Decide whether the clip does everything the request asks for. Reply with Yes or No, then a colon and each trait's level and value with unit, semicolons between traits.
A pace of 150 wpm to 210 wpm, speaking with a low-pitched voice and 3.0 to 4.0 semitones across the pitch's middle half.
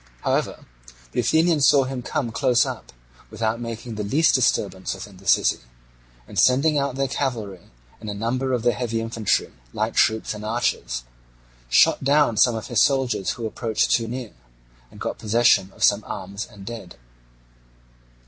Yes: average, 165 wpm; low, 115 Hz; average, 3.6 semitones